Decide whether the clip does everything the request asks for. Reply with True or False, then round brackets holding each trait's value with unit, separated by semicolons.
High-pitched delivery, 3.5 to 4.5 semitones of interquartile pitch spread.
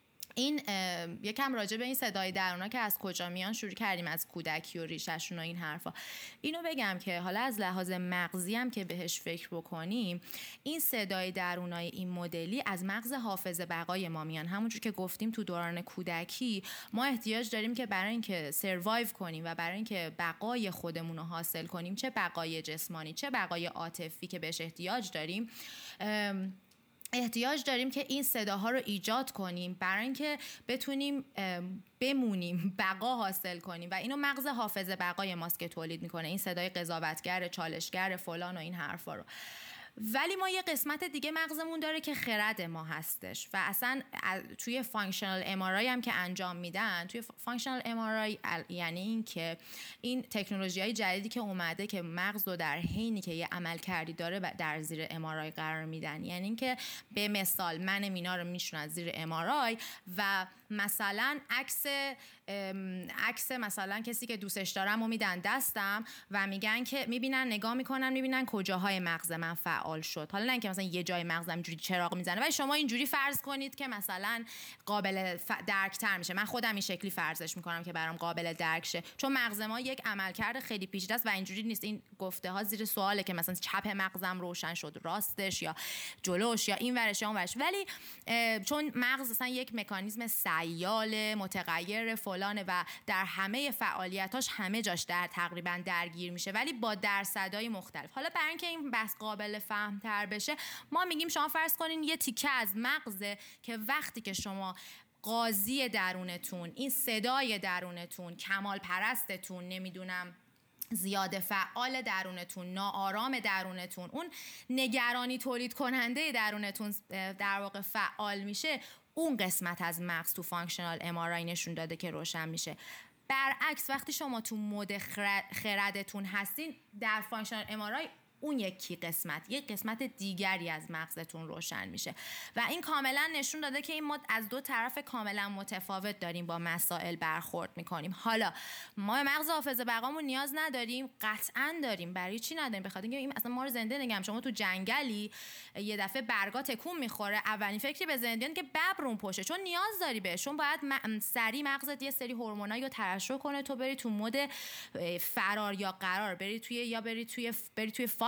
False (205 Hz; 5.4 semitones)